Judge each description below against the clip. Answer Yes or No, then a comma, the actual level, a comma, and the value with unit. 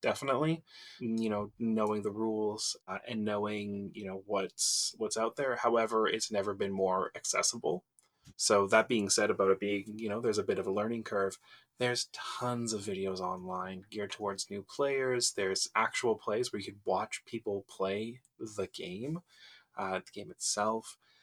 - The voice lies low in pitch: Yes, low, 105 Hz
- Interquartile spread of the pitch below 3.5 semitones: Yes, average, 2.8 semitones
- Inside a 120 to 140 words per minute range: No, average, 170 wpm